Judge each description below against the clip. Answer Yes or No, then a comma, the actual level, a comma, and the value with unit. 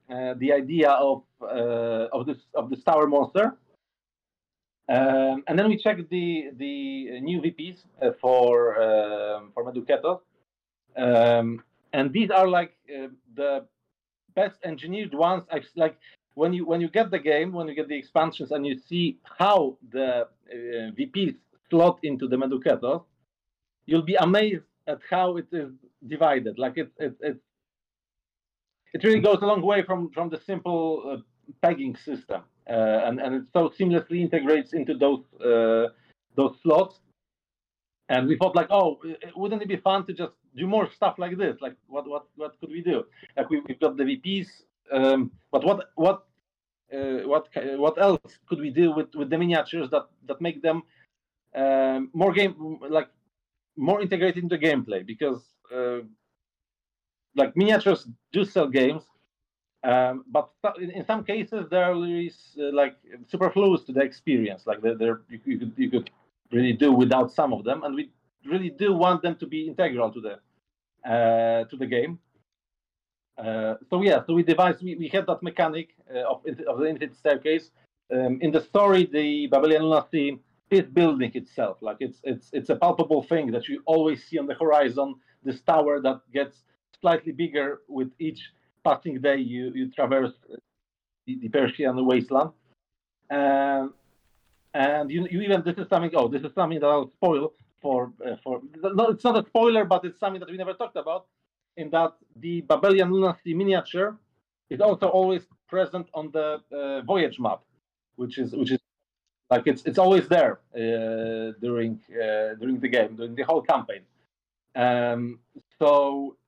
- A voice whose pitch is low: No, medium, 155 Hz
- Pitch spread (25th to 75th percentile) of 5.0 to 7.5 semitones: Yes, wide, 5.5 semitones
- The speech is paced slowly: No, average, 170 wpm